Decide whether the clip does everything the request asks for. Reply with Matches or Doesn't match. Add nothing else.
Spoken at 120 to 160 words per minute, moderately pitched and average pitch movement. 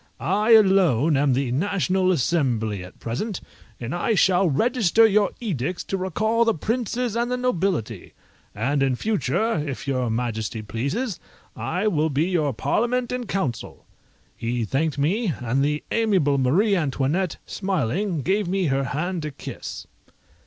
Doesn't match